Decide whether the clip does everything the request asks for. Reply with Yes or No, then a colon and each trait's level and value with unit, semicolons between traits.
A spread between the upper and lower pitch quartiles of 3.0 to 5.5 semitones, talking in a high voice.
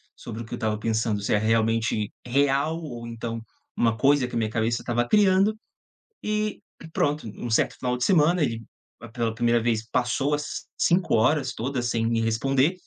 No: average, 4.1 semitones; low, 120 Hz